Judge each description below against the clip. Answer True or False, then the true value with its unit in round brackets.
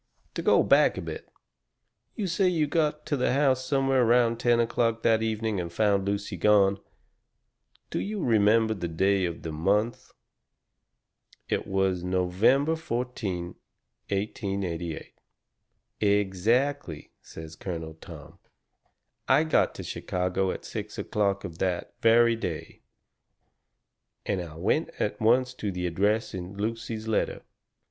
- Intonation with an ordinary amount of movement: True (4.5 semitones)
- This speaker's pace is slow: True (130 wpm)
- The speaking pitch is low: True (105 Hz)